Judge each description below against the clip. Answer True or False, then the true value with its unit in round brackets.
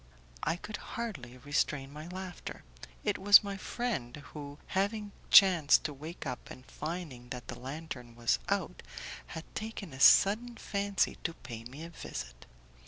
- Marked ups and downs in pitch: True (7.3 semitones)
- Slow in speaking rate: False (155 wpm)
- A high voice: False (160 Hz)